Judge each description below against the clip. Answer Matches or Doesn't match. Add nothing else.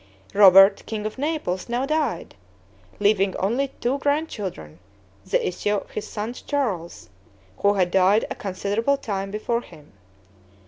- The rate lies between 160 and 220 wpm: Doesn't match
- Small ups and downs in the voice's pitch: Doesn't match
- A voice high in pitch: Matches